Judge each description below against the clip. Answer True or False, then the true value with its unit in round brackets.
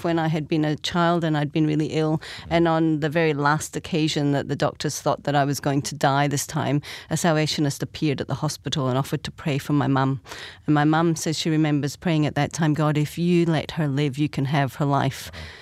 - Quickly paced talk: True (240 wpm)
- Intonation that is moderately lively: False (1.9 semitones)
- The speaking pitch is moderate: True (150 Hz)